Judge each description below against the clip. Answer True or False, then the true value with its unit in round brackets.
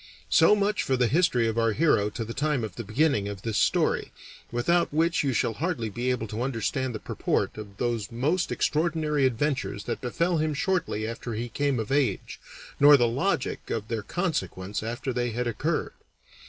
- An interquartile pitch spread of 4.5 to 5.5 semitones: True (5.1 semitones)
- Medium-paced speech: True (190 wpm)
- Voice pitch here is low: True (125 Hz)